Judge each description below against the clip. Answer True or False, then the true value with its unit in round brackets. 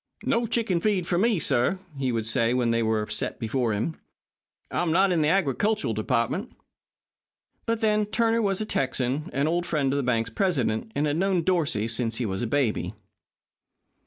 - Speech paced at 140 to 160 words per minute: False (180 wpm)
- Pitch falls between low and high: True (150 Hz)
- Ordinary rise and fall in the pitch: False (8.7 semitones)